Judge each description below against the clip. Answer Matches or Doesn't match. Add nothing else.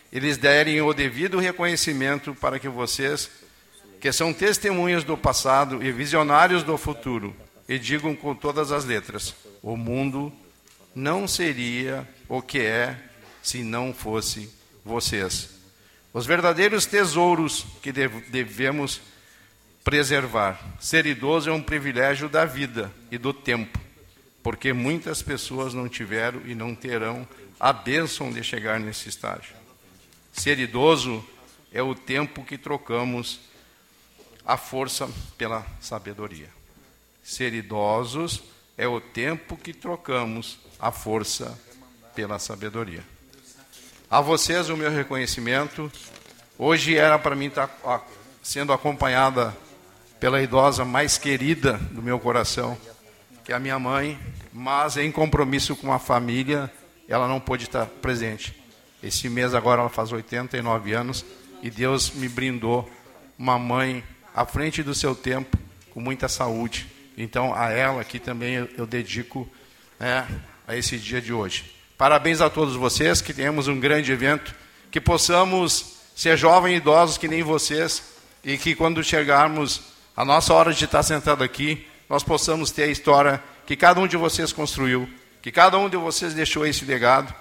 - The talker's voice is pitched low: Matches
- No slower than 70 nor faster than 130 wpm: Doesn't match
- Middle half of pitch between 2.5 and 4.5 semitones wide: Matches